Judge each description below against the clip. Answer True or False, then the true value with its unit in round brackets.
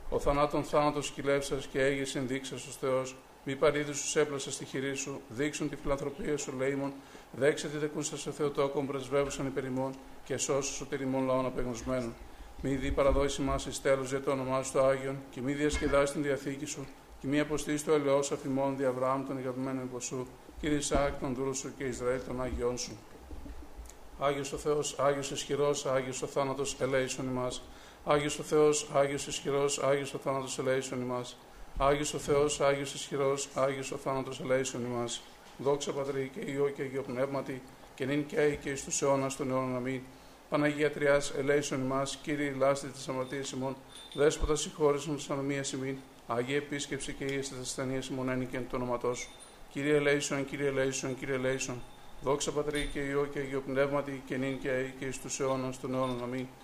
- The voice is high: False (140 Hz)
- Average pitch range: False (1.4 semitones)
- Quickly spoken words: True (180 wpm)